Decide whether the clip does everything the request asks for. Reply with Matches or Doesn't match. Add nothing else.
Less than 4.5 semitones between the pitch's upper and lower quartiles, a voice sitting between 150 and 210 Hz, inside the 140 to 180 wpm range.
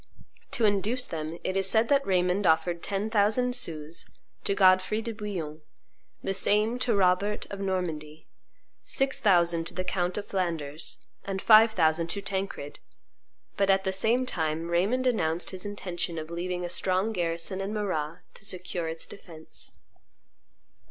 Matches